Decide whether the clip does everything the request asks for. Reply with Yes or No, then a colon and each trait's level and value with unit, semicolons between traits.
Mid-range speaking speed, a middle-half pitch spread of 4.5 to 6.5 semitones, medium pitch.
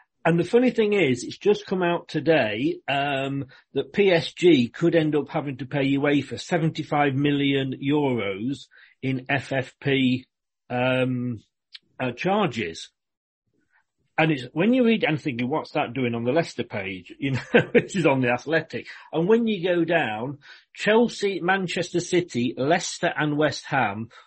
Yes: average, 150 wpm; average, 5.2 semitones; medium, 145 Hz